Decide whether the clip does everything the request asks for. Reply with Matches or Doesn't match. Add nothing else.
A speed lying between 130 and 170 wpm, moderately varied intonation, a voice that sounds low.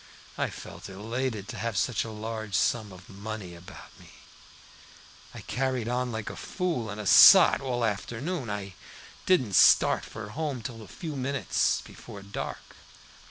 Matches